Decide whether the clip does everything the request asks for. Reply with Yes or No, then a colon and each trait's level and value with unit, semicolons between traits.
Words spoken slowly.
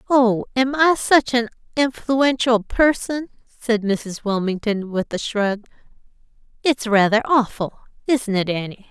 Yes: slow, 120 wpm